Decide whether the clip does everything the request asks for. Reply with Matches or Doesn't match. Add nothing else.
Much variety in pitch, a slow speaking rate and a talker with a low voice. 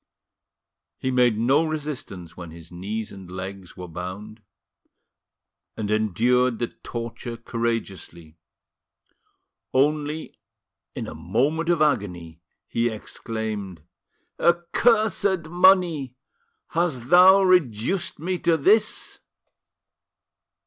Matches